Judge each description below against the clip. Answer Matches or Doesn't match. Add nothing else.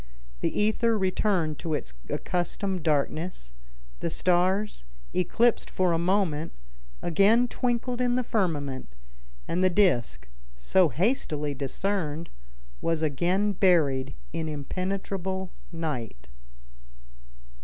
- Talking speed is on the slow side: Matches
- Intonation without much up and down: Doesn't match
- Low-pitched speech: Doesn't match